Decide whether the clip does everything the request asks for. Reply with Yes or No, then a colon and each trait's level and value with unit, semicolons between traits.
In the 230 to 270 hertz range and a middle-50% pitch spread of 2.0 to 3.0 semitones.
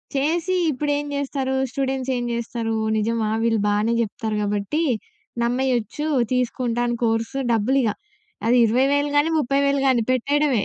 No: very high, 255 Hz; average, 3.5 semitones